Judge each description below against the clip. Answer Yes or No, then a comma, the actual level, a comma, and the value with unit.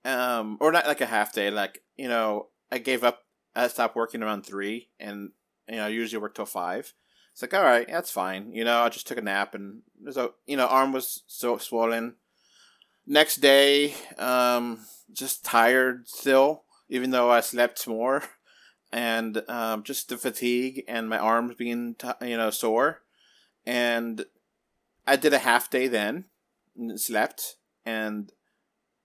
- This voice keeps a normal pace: Yes, average, 165 wpm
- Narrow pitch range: Yes, narrow, 1.8 semitones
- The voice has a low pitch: Yes, low, 120 Hz